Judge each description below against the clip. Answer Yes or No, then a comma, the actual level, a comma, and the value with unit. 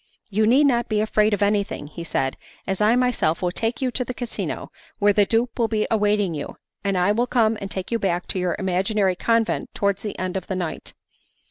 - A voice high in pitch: Yes, high, 210 Hz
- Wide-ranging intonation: No, average, 3.3 semitones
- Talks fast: Yes, fast, 225 wpm